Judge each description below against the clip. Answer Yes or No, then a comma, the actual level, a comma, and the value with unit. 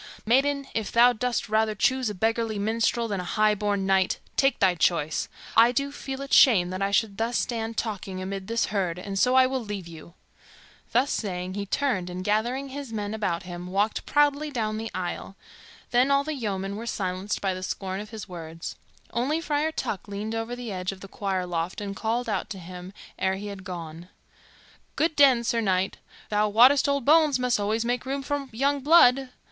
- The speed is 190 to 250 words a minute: Yes, average, 200 wpm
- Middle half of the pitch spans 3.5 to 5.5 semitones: Yes, average, 4.7 semitones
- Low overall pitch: No, high, 215 Hz